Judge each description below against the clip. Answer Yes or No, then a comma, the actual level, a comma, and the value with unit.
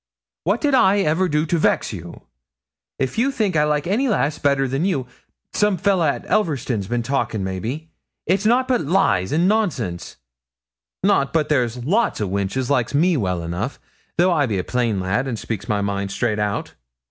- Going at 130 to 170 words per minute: No, average, 185 wpm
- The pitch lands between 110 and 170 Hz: Yes, medium, 140 Hz